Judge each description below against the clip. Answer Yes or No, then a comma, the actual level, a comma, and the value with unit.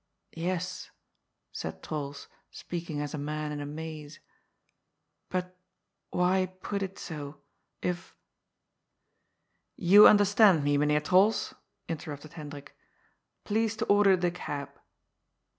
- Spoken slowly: Yes, slow, 125 wpm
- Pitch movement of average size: Yes, average, 4.0 semitones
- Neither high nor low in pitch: Yes, medium, 165 Hz